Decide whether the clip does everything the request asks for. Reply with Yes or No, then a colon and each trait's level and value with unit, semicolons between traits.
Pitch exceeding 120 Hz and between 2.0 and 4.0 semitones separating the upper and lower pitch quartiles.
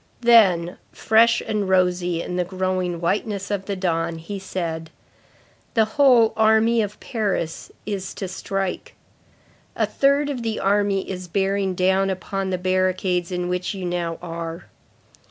Yes: high, 190 Hz; average, 2.7 semitones